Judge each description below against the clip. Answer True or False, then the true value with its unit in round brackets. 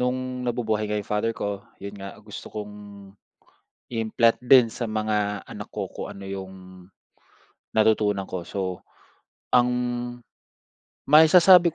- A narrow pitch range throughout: False (3.3 semitones)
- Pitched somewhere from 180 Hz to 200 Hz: False (110 Hz)